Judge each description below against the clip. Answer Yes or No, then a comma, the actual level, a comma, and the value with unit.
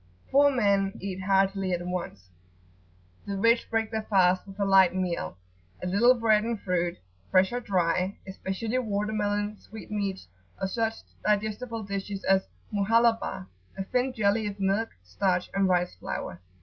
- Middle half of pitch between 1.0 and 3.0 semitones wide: Yes, average, 2.7 semitones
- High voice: Yes, high, 200 Hz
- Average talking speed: Yes, average, 150 wpm